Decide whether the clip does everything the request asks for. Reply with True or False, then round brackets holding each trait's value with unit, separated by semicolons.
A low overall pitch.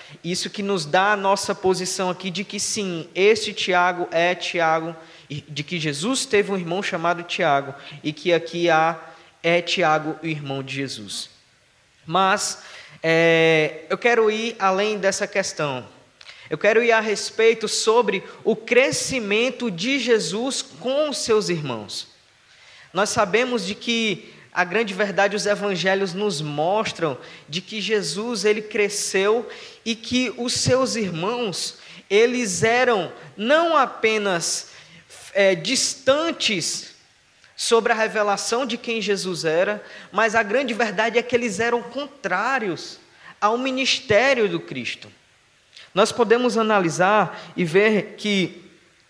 False (200 Hz)